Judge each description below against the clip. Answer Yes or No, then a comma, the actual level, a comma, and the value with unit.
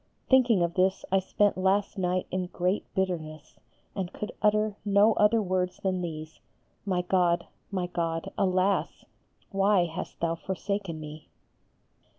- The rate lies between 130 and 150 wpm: Yes, average, 140 wpm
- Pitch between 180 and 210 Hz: Yes, medium, 185 Hz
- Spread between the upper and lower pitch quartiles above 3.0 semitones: No, narrow, 2.4 semitones